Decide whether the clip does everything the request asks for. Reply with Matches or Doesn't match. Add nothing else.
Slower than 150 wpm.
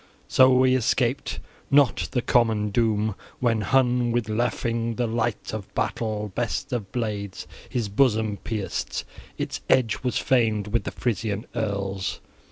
Matches